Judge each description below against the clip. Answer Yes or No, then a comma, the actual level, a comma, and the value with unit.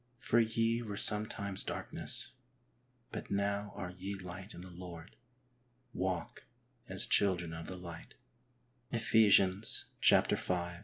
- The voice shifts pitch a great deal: No, average, 3.4 semitones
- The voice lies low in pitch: Yes, low, 100 Hz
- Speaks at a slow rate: Yes, slow, 120 wpm